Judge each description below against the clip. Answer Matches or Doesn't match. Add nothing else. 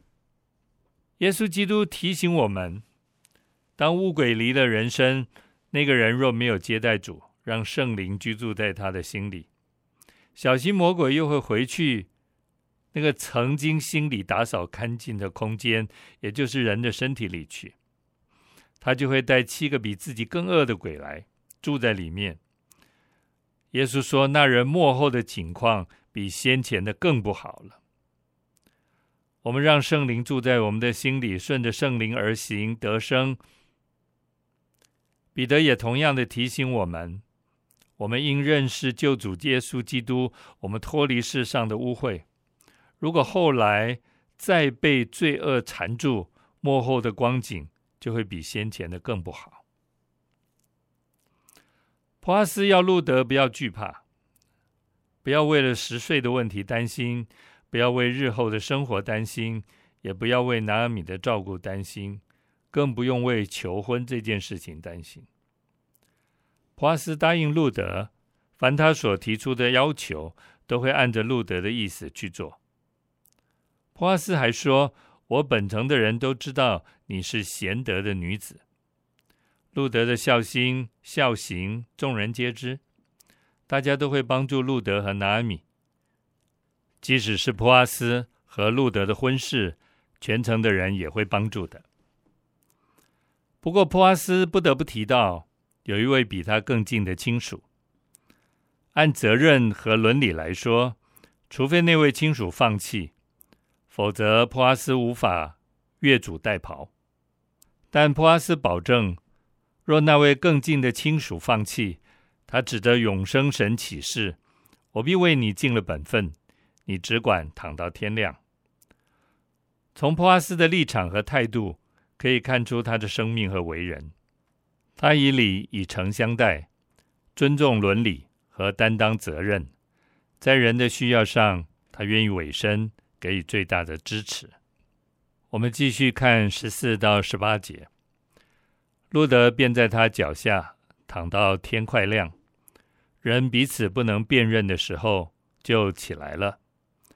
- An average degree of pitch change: Matches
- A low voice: Matches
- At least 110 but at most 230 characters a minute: Matches